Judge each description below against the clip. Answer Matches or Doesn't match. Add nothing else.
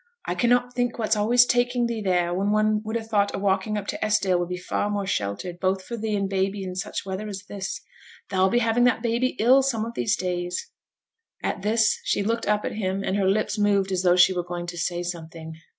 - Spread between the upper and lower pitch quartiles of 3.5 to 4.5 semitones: Doesn't match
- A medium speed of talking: Doesn't match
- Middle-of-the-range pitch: Doesn't match